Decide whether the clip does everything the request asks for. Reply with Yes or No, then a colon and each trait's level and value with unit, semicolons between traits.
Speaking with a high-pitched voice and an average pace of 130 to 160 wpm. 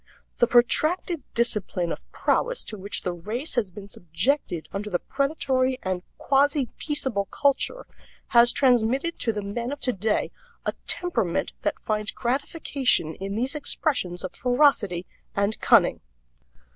Yes: high, 235 Hz; slow, 135 wpm